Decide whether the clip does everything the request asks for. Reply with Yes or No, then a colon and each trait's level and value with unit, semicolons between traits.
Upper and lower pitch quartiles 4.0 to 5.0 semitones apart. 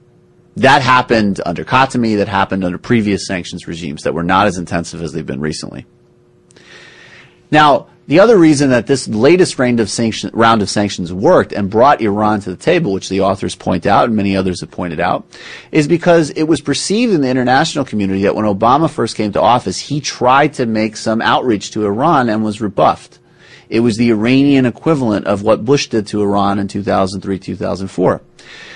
Yes: average, 4.7 semitones